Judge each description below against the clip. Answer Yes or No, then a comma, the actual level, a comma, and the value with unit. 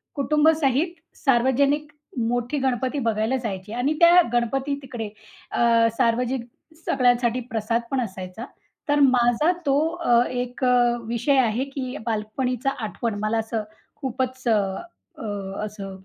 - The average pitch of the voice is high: Yes, high, 245 Hz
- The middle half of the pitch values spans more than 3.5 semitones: No, average, 2.9 semitones